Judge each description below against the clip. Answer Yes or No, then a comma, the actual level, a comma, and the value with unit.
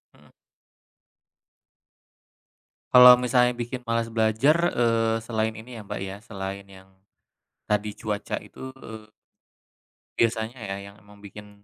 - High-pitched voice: No, low, 110 Hz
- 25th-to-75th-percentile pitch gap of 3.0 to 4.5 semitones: No, narrow, 2.6 semitones